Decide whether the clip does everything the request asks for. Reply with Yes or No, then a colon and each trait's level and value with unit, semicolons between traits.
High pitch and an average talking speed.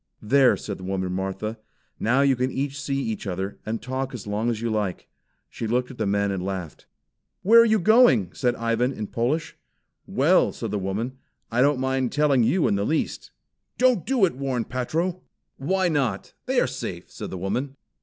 No: low, 125 Hz; average, 195 wpm